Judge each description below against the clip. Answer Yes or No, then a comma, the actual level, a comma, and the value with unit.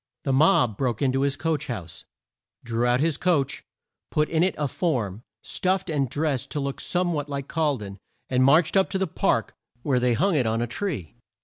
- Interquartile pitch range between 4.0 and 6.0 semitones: Yes, average, 4.8 semitones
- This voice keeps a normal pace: No, fast, 210 wpm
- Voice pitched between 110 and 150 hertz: Yes, medium, 140 Hz